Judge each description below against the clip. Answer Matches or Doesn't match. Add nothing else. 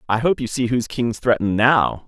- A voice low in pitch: Matches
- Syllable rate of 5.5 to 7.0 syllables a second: Matches